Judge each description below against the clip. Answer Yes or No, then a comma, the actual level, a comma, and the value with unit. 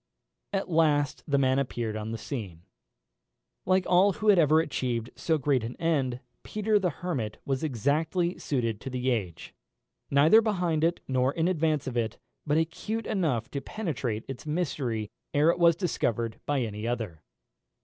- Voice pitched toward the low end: No, medium, 145 Hz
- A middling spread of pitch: No, wide, 6.0 semitones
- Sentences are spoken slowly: No, average, 165 wpm